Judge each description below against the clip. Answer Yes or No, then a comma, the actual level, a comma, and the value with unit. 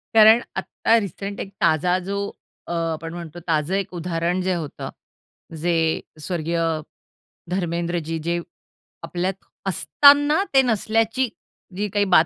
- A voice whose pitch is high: No, medium, 180 Hz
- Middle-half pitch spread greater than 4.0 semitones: No, average, 3.6 semitones